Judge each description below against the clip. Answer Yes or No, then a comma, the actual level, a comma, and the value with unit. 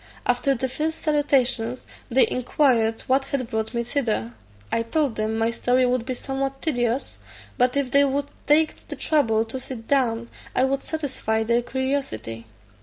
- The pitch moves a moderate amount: Yes, average, 3.3 semitones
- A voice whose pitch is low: No, very high, 255 Hz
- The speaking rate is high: No, average, 165 wpm